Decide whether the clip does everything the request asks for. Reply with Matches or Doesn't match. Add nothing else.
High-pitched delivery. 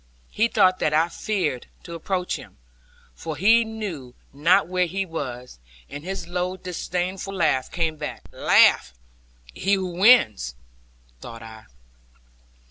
Doesn't match